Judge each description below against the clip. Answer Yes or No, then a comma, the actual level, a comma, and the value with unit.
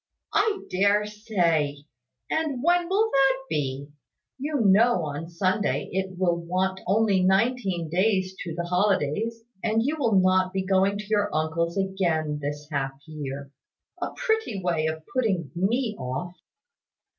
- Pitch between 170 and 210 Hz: Yes, high, 190 Hz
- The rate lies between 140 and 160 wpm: Yes, average, 145 wpm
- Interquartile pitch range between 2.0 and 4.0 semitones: No, average, 5.0 semitones